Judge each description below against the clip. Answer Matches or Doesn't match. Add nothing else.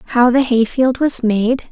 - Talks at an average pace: Doesn't match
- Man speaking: Doesn't match